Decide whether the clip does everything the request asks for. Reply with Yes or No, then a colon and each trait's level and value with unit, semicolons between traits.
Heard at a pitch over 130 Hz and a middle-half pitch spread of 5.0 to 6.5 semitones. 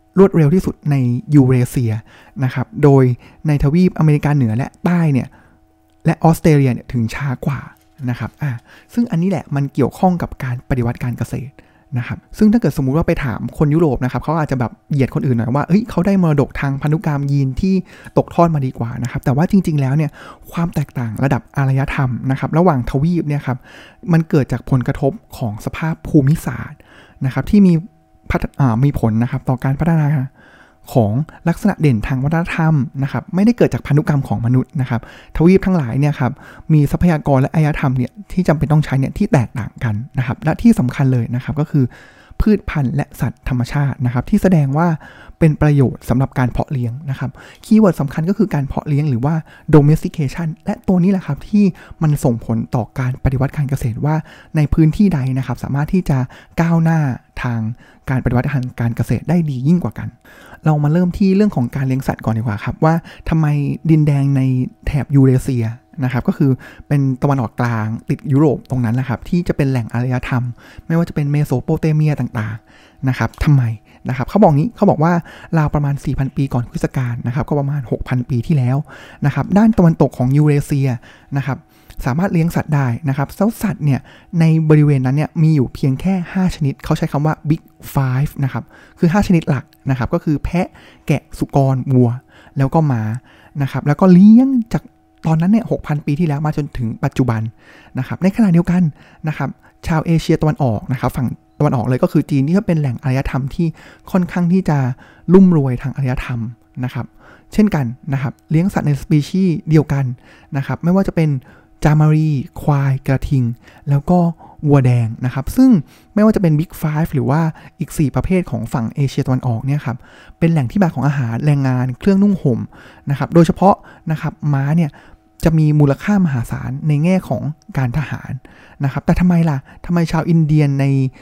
No: medium, 140 Hz; average, 4.3 semitones